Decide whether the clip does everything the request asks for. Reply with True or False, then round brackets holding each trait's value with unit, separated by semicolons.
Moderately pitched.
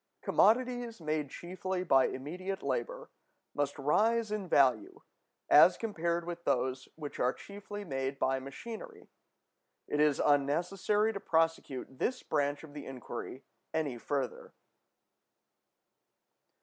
True (160 Hz)